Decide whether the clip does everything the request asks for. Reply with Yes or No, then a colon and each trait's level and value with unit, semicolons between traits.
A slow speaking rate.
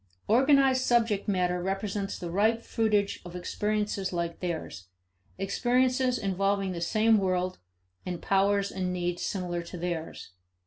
Yes: slow, 130 wpm